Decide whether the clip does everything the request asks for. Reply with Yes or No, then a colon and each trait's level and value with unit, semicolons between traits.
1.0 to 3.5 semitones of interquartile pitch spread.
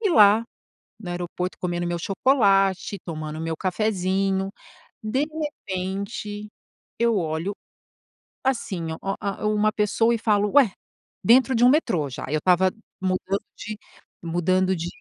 Yes: average, 3.2 semitones